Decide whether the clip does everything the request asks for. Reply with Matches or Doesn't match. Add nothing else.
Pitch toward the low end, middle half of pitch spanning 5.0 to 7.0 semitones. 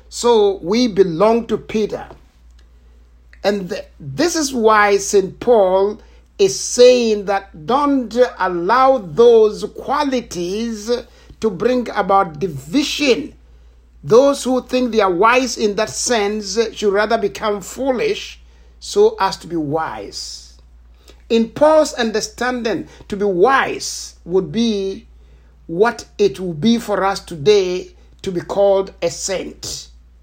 Doesn't match